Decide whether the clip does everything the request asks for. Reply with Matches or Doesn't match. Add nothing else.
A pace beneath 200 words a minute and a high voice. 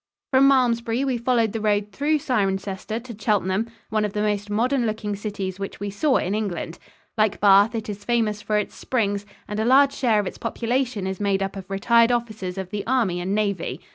Doesn't match